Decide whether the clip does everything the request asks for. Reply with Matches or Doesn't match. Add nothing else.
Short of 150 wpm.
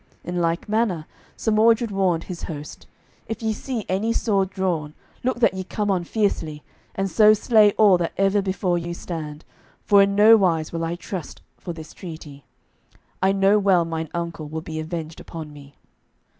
Doesn't match